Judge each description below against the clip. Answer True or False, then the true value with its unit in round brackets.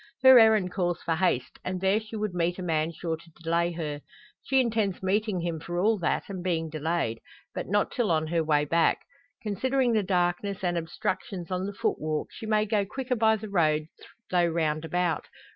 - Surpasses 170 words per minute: True (195 wpm)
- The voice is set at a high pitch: False (180 Hz)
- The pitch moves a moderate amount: True (4.2 semitones)